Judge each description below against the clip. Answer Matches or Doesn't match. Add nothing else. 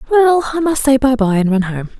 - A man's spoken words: Doesn't match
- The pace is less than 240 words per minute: Doesn't match